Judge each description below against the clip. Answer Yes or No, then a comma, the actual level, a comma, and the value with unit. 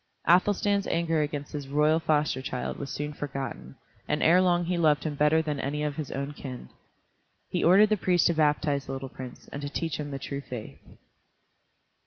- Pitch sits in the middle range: Yes, medium, 150 Hz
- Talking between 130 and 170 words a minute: No, average, 195 wpm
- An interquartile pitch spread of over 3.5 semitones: No, average, 2.9 semitones